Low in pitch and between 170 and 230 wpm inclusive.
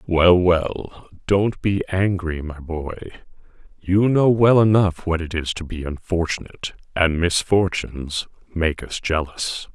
No: very low, 90 Hz; slow, 135 wpm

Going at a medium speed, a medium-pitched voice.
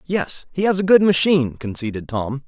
Yes: average, 195 wpm; medium, 155 Hz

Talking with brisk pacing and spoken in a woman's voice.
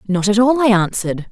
Yes: fast, 230 wpm; female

